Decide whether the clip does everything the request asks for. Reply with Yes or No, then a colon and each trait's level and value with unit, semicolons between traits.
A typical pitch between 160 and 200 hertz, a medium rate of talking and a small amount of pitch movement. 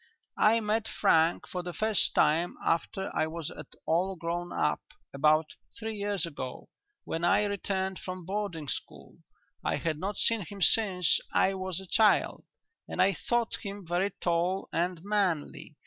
No: medium, 185 Hz; average, 160 wpm; average, 3.3 semitones